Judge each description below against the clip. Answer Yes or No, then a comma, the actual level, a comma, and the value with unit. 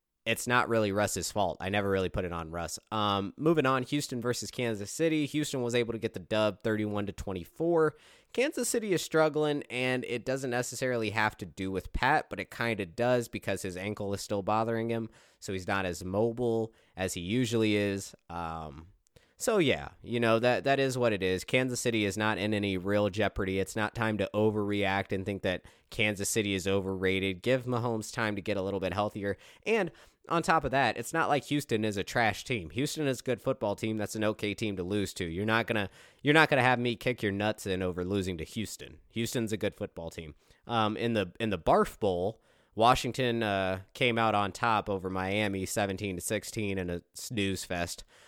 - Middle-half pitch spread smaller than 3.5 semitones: No, average, 3.8 semitones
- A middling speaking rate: No, fast, 215 wpm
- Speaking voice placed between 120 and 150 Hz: No, low, 105 Hz